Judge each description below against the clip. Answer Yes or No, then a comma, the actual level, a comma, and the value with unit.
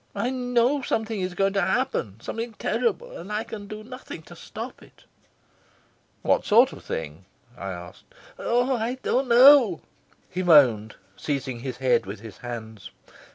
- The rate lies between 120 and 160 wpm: Yes, average, 155 wpm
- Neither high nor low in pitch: No, high, 200 Hz